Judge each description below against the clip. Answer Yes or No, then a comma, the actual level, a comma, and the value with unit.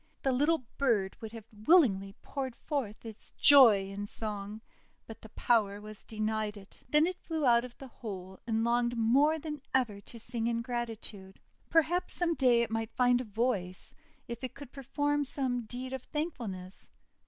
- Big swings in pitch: No, average, 4.1 semitones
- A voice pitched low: No, high, 235 Hz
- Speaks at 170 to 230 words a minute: Yes, average, 175 wpm